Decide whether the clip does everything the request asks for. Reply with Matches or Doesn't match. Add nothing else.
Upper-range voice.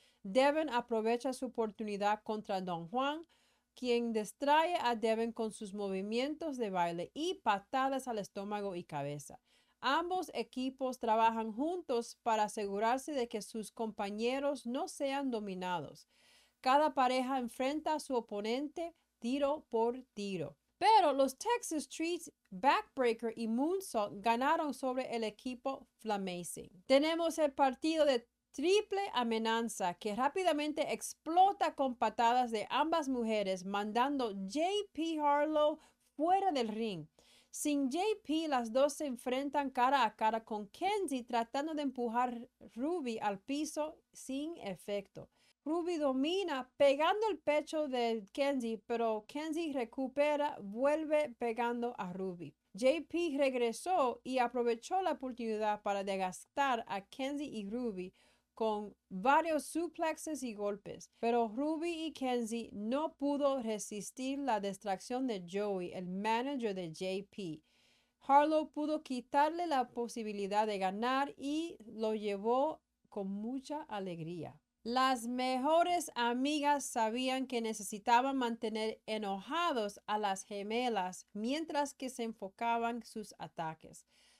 Matches